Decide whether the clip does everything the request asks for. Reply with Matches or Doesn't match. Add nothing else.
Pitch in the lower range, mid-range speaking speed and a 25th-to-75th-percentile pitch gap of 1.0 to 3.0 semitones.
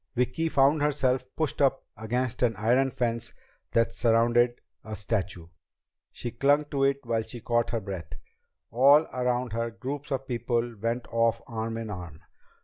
Matches